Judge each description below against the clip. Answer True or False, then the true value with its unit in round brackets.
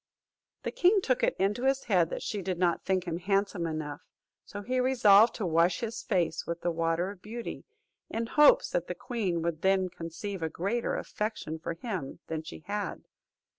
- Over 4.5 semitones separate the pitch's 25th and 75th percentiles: True (5.0 semitones)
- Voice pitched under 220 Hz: True (190 Hz)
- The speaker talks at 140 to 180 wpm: False (190 wpm)